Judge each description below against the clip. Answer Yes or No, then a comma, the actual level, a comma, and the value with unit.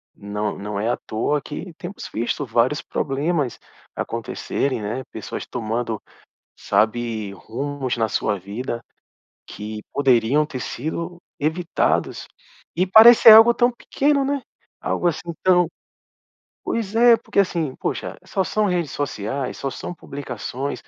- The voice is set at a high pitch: No, medium, 140 Hz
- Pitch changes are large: Yes, wide, 7.6 semitones